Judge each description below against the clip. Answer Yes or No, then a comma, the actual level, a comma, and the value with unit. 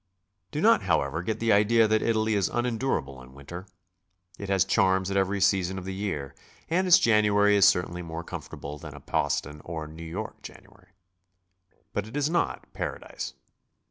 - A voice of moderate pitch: No, very low, 95 Hz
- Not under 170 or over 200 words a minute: Yes, average, 175 wpm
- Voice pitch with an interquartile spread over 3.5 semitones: Yes, average, 4.7 semitones